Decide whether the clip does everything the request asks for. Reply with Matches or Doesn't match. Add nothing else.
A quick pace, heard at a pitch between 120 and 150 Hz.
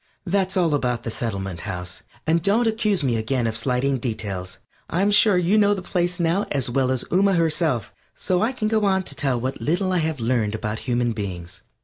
Matches